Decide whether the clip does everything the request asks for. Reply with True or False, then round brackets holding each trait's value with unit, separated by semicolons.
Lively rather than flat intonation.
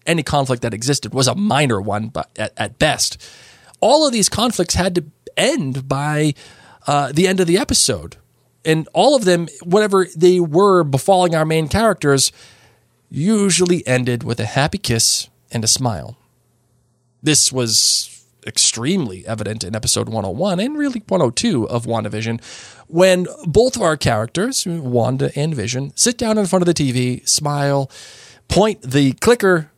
True (7.3 semitones)